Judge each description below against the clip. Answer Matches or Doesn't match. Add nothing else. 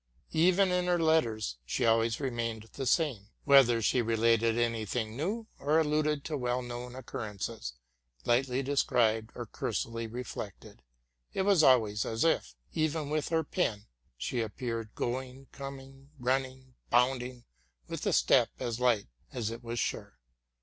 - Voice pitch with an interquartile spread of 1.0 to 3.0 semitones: Doesn't match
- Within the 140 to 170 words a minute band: Matches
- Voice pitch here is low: Matches